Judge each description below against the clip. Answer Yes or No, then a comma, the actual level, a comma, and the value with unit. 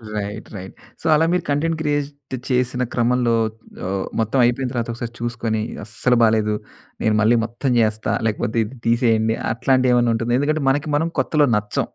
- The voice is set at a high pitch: No, low, 120 Hz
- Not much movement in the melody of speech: No, average, 3.3 semitones